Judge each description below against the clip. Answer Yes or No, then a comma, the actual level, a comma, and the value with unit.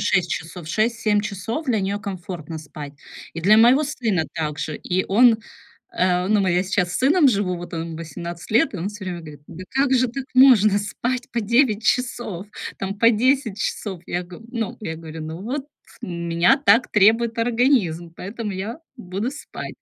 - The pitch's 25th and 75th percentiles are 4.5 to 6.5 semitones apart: Yes, average, 5.1 semitones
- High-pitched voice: Yes, high, 200 Hz